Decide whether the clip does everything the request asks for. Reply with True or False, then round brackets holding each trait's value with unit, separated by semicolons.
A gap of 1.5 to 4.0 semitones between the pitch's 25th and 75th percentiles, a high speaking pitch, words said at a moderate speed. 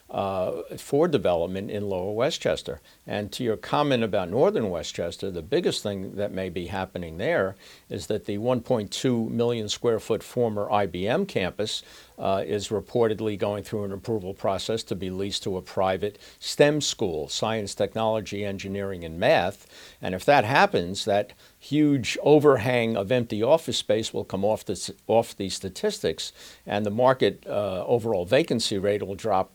False (3.1 semitones; 105 Hz; 155 wpm)